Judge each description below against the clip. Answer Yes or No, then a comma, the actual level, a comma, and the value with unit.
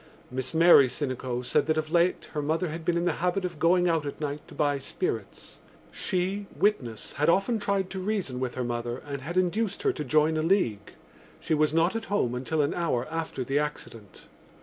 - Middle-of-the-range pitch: Yes, medium, 155 Hz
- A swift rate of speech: Yes, fast, 210 wpm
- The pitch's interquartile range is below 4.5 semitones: No, average, 5.2 semitones